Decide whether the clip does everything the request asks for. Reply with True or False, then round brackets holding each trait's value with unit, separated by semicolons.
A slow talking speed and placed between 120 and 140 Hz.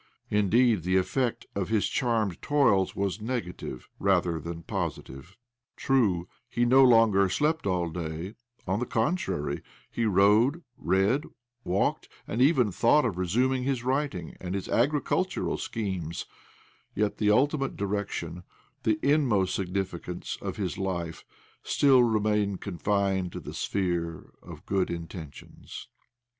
False (130 wpm; 100 Hz)